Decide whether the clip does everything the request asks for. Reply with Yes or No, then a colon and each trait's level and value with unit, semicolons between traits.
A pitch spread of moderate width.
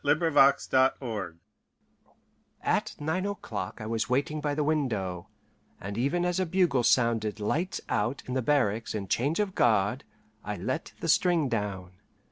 No: wide, 6.6 semitones